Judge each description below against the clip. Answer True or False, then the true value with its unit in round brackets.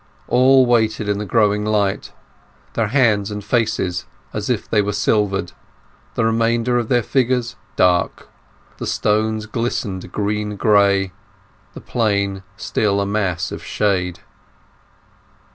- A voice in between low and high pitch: False (105 Hz)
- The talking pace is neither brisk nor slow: False (125 wpm)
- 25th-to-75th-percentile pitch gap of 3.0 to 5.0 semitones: False (2.4 semitones)